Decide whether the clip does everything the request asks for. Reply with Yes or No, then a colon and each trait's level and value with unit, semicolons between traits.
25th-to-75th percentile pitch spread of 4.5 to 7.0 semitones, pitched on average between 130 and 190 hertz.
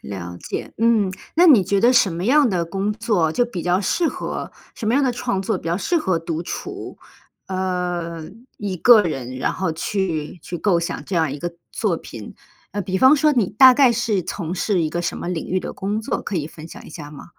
Yes: average, 5.0 semitones; medium, 185 Hz